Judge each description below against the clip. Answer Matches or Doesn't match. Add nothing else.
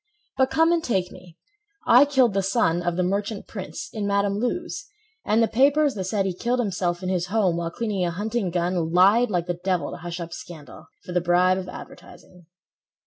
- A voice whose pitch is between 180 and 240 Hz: Matches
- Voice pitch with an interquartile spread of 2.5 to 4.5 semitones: Matches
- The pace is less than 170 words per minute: Doesn't match